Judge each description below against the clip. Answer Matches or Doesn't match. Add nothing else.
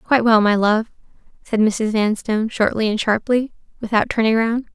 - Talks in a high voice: Matches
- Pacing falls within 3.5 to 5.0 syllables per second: Doesn't match